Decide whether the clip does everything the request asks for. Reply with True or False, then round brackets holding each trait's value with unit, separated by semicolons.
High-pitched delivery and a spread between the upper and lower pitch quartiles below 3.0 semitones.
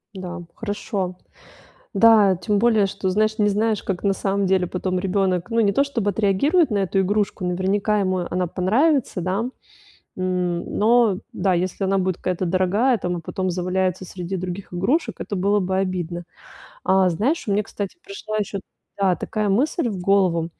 True (195 Hz; 2.5 semitones)